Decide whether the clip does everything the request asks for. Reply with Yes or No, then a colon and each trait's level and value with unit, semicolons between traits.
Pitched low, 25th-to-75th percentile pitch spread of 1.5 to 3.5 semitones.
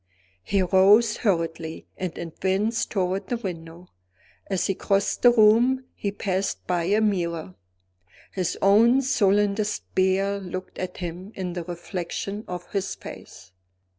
No: high, 190 Hz; average, 2.7 semitones